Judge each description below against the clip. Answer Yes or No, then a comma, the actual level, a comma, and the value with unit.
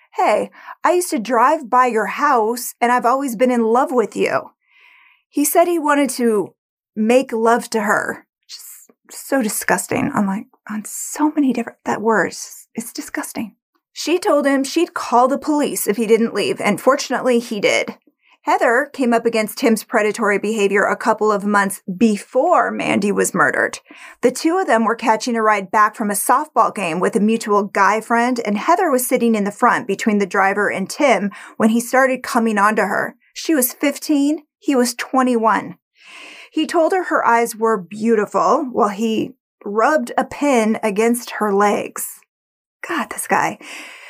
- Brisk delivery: No, average, 175 wpm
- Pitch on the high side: Yes, high, 235 Hz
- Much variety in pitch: No, average, 4.6 semitones